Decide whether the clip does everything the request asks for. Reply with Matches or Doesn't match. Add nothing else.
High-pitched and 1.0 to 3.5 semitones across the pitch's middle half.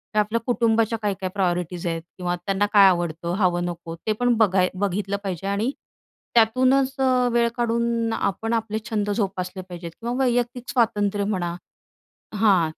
Doesn't match